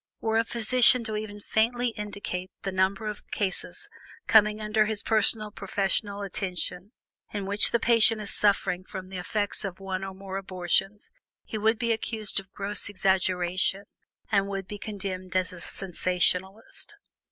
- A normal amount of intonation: No, narrow, 2.3 semitones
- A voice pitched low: No, high, 200 Hz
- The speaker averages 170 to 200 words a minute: No, average, 155 wpm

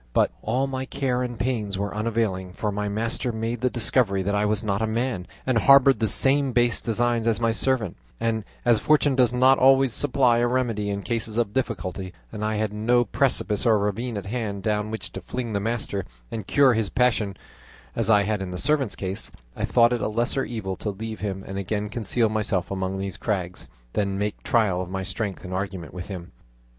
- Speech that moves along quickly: Yes, fast, 210 wpm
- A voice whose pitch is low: Yes, low, 110 Hz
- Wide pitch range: No, average, 3.3 semitones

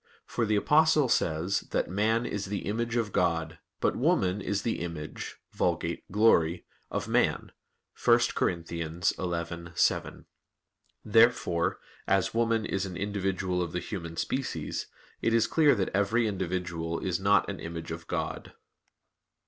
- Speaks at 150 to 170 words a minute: No, average, 140 wpm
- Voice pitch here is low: Yes, very low, 95 Hz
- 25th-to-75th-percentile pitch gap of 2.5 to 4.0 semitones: No, average, 4.4 semitones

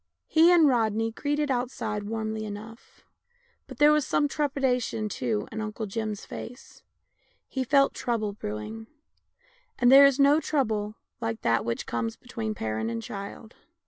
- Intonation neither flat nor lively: Yes, average, 4.5 semitones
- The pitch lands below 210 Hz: No, high, 225 Hz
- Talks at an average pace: Yes, average, 150 wpm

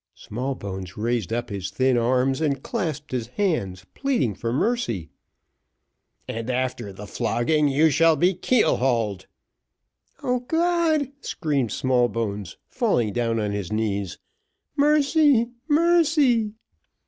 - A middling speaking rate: No, slow, 115 wpm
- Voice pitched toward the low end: Yes, low, 130 Hz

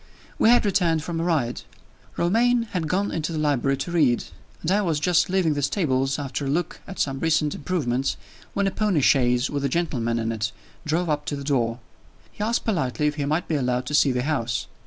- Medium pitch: Yes, medium, 150 Hz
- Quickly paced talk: Yes, fast, 220 wpm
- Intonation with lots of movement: No, average, 4.6 semitones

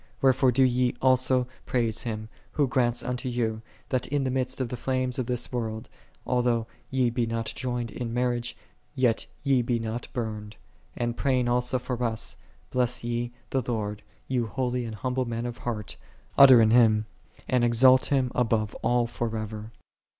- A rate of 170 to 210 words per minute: Yes, average, 180 wpm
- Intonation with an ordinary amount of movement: No, narrow, 1.8 semitones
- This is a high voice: No, low, 120 Hz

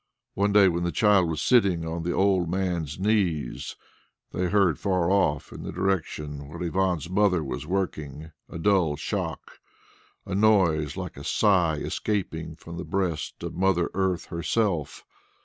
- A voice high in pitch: No, very low, 90 Hz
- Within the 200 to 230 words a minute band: No, average, 155 wpm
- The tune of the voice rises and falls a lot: No, average, 3.3 semitones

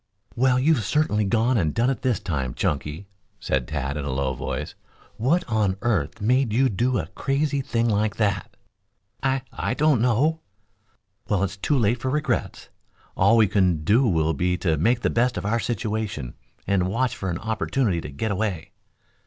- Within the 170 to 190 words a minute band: Yes, average, 180 wpm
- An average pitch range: No, wide, 5.8 semitones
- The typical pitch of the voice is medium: No, low, 110 Hz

